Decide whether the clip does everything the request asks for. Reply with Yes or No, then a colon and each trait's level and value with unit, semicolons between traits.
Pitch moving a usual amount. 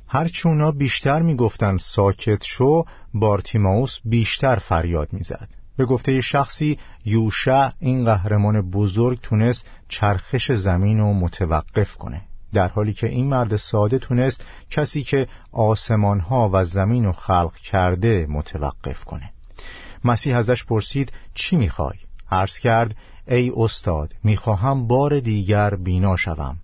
Yes: average, 4.8 semitones